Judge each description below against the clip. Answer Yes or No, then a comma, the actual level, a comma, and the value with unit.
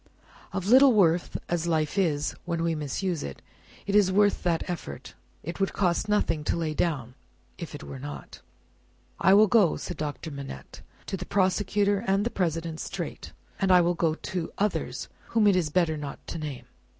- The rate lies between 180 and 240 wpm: Yes, average, 185 wpm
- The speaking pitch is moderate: Yes, medium, 175 Hz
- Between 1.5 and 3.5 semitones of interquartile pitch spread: No, average, 4.0 semitones